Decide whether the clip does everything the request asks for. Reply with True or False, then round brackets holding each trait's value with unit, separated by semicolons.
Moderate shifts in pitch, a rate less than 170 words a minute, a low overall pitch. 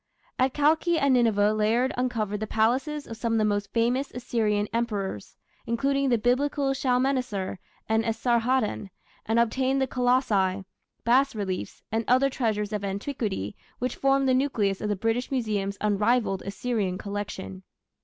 False (3.8 semitones; 145 wpm; 230 Hz)